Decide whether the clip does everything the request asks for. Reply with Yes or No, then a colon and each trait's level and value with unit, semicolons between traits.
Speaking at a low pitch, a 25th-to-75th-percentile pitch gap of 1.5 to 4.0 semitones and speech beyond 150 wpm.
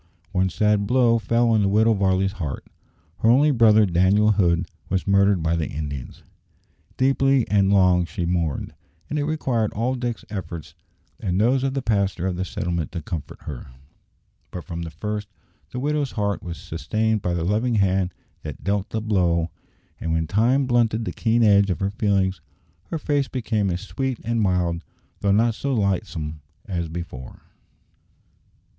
No: low, 100 Hz; average, 4.6 semitones; average, 170 wpm